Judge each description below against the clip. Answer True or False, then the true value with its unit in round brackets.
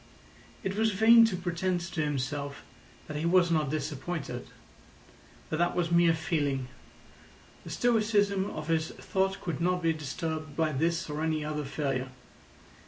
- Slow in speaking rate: False (150 wpm)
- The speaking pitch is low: False (165 Hz)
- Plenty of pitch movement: False (3.4 semitones)